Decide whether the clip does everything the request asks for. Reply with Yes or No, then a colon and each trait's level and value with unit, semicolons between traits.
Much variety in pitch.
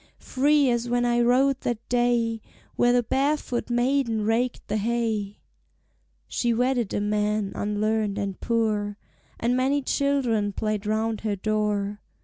No: average, 2.7 semitones